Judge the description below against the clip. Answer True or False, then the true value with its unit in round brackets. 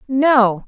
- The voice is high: True (245 Hz)